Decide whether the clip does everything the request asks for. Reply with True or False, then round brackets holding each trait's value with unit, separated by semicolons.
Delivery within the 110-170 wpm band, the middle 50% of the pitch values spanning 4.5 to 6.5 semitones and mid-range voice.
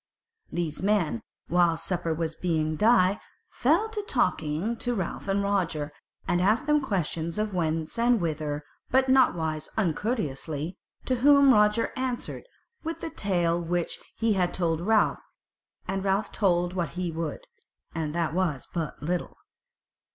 True (145 wpm; 5.0 semitones; 180 Hz)